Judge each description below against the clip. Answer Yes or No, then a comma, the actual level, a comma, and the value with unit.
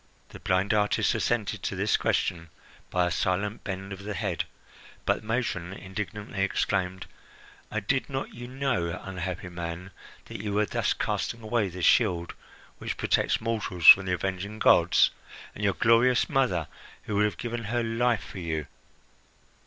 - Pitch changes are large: No, average, 3.7 semitones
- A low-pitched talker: Yes, low, 100 Hz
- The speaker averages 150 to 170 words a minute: Yes, average, 160 wpm